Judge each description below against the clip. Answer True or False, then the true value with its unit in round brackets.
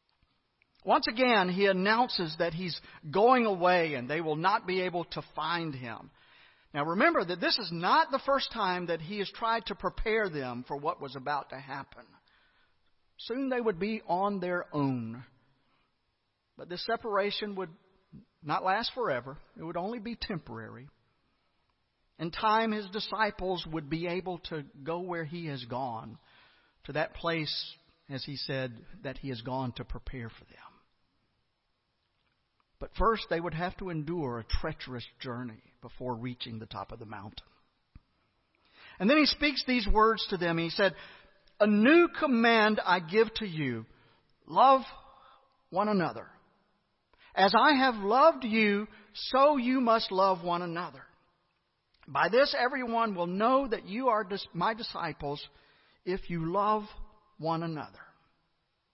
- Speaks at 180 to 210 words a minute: False (150 wpm)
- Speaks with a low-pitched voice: False (180 Hz)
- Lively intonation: True (7.3 semitones)